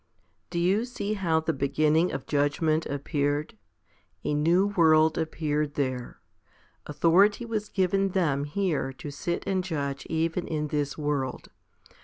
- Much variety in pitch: No, average, 3.9 semitones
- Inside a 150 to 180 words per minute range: No, average, 140 wpm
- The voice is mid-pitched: Yes, medium, 160 Hz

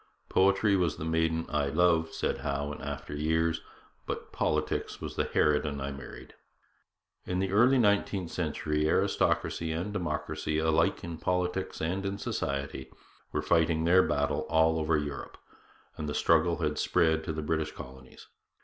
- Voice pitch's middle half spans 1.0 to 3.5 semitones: Yes, average, 2.8 semitones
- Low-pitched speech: Yes, very low, 80 Hz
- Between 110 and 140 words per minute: No, average, 155 wpm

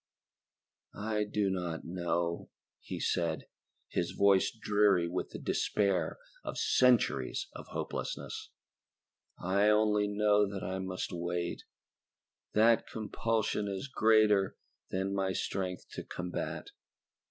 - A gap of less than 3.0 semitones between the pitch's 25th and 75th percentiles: Yes, narrow, 2.6 semitones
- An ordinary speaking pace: No, slow, 110 wpm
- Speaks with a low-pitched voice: Yes, low, 100 Hz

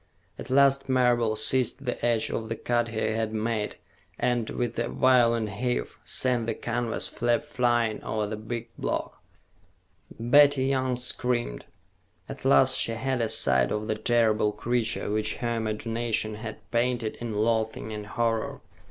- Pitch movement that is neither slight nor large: No, narrow, 2.1 semitones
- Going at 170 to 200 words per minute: No, average, 150 wpm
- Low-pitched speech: Yes, low, 115 Hz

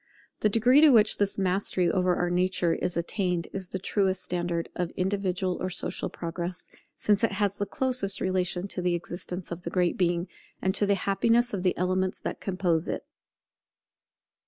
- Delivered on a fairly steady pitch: Yes, narrow, 2.0 semitones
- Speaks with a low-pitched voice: No, medium, 185 Hz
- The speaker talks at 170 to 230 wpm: Yes, average, 180 wpm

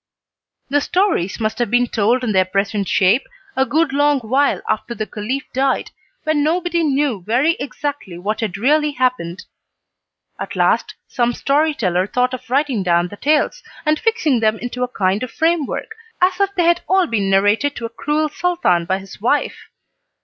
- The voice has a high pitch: Yes, very high, 255 Hz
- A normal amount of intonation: No, wide, 6.1 semitones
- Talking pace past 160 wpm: Yes, average, 175 wpm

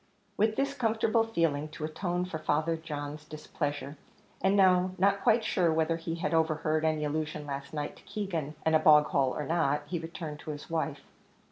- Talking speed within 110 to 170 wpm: No, average, 190 wpm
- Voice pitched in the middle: Yes, medium, 160 Hz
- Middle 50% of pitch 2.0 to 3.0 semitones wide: No, average, 3.4 semitones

